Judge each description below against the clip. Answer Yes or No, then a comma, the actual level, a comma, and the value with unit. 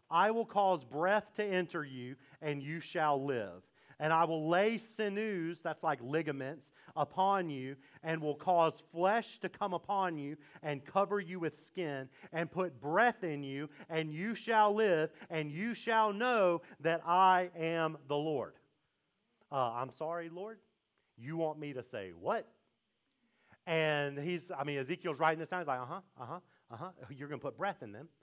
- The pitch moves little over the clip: No, average, 4.3 semitones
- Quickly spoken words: No, average, 180 wpm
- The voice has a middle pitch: Yes, medium, 165 Hz